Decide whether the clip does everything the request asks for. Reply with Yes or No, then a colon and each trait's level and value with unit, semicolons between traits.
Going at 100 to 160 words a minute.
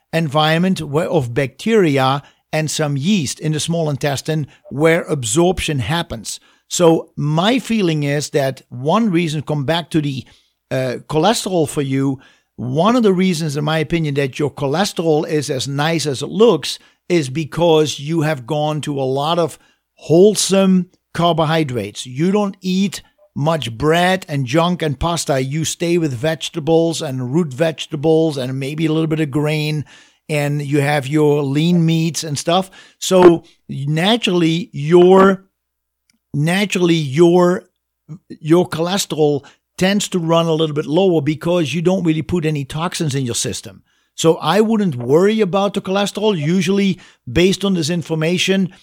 Yes: average, 150 wpm